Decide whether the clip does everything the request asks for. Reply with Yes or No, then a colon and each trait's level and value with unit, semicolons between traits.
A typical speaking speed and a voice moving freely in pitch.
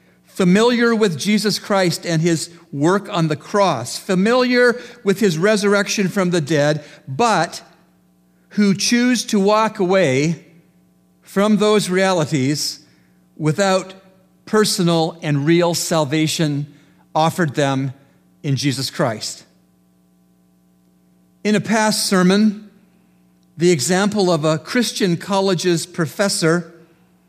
No: slow, 105 wpm; wide, 5.9 semitones